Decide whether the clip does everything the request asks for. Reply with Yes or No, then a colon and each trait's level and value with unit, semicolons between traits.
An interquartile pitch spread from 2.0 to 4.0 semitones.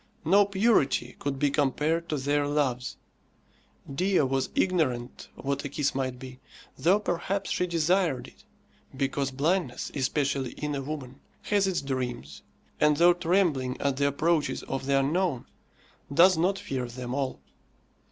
No: average, 4.4 semitones